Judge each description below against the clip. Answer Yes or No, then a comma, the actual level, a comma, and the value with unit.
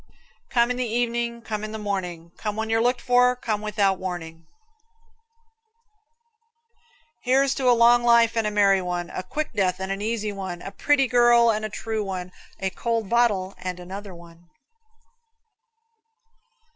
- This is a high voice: Yes, high, 215 Hz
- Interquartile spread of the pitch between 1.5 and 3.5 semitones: No, average, 3.9 semitones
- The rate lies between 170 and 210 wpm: No, average, 160 wpm